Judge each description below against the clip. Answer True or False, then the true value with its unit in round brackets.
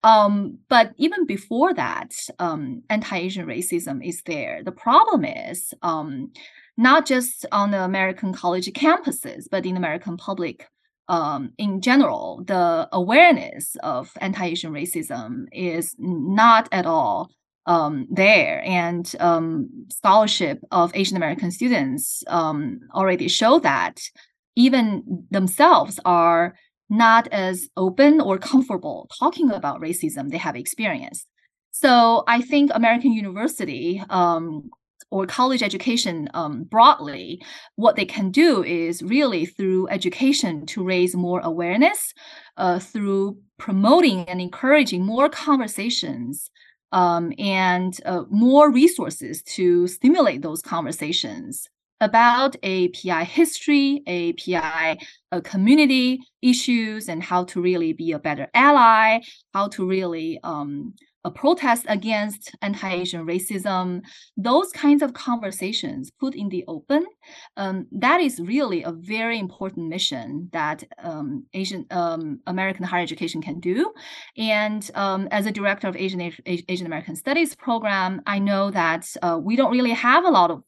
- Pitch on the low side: False (205 Hz)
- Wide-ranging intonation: True (7.0 semitones)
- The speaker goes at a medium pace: False (130 wpm)